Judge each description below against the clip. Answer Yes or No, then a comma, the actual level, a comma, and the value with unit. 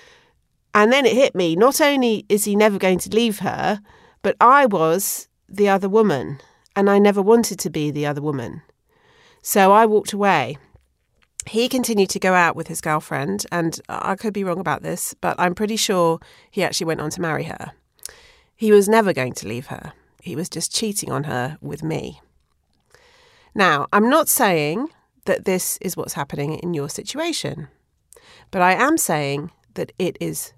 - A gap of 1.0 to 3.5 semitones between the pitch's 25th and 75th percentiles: No, wide, 5.4 semitones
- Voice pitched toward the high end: Yes, high, 200 Hz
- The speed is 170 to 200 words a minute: Yes, average, 180 wpm